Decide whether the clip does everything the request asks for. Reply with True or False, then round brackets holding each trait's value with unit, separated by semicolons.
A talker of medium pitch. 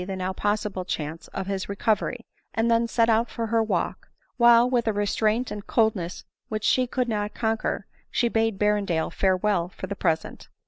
False (210 Hz)